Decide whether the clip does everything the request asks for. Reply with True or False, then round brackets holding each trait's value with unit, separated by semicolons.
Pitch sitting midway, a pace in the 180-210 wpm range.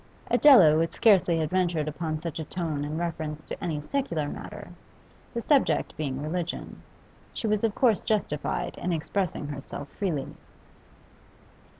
False (165 Hz; 140 wpm)